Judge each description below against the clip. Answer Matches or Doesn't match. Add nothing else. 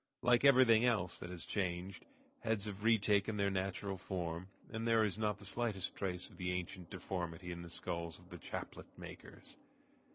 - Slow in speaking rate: Doesn't match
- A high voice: Doesn't match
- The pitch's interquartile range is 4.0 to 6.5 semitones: Doesn't match